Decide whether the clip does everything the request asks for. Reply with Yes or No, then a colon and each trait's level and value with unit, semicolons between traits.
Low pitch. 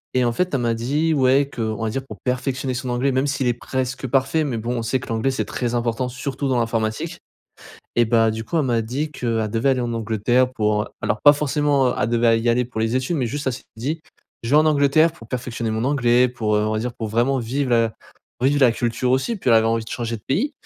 Yes: low, 125 Hz